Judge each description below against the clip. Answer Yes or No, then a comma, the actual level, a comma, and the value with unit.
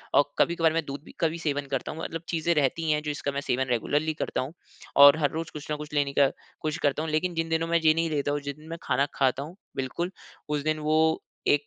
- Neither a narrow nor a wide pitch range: No, narrow, 2.3 semitones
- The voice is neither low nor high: Yes, medium, 150 Hz